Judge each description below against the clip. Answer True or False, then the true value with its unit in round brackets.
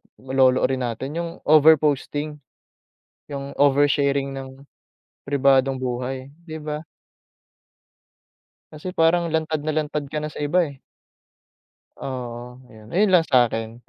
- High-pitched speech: False (140 Hz)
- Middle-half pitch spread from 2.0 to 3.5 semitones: True (2.8 semitones)